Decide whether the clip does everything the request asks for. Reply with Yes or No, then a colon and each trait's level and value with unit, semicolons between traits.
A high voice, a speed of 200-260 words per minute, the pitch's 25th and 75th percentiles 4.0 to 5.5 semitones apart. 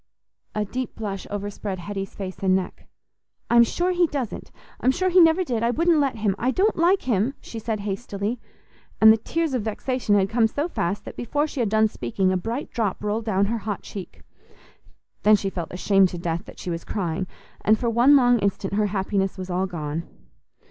Yes: high, 215 Hz; fast, 205 wpm; average, 4.5 semitones